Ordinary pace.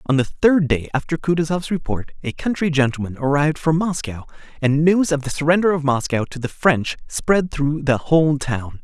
Yes: average, 190 wpm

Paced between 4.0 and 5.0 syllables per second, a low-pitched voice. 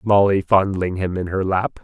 Yes: 4.7 syllables/s; very low, 95 Hz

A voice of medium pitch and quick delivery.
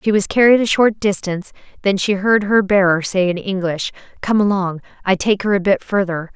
No: high, 195 Hz; fast, 210 wpm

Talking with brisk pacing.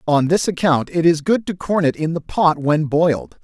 Yes: fast, 245 wpm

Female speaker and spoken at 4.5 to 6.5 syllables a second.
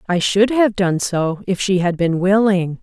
No: female; 4.3 syllables/s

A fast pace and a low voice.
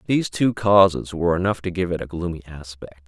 Yes: fast, 215 wpm; very low, 90 Hz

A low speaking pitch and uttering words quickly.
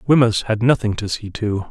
Yes: low, 110 Hz; fast, 210 wpm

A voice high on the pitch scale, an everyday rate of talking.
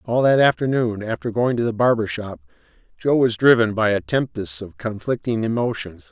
No: low, 115 Hz; average, 175 wpm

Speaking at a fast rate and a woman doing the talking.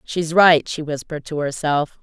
No: average, 180 wpm; female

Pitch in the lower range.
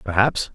Yes: low, 105 Hz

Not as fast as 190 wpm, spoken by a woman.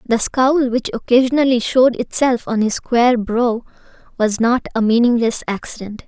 Yes: average, 150 wpm; female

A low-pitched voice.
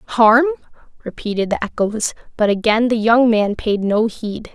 No: high, 220 Hz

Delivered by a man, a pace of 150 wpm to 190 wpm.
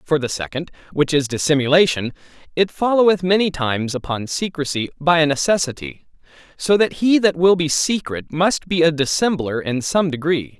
Yes: male; average, 165 wpm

